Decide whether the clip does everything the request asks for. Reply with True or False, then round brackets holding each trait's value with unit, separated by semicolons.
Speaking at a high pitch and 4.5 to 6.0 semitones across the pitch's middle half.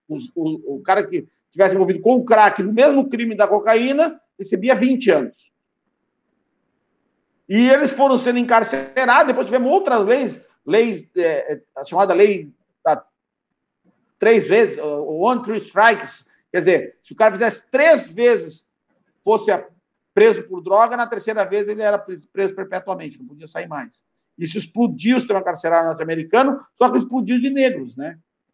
True (230 Hz; 5.6 semitones)